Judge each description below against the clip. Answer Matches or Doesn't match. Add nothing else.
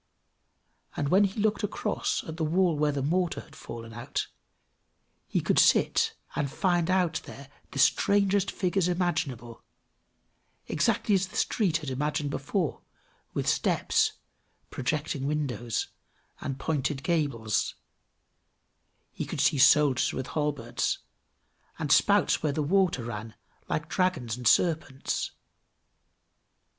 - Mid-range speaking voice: Matches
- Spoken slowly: Matches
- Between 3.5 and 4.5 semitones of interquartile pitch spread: Doesn't match